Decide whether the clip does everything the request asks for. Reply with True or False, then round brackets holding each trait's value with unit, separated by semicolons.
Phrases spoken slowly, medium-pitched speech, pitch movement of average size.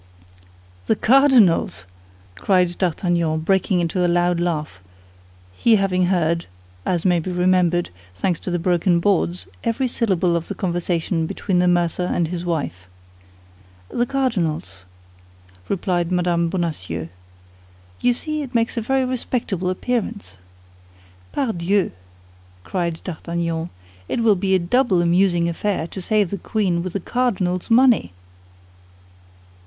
True (125 wpm; 180 Hz; 3.1 semitones)